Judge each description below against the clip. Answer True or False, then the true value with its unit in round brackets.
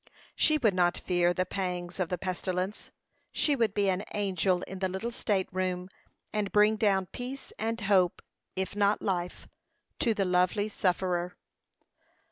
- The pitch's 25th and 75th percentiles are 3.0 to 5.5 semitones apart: False (2.5 semitones)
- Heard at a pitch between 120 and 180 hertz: False (190 Hz)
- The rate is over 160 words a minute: False (155 wpm)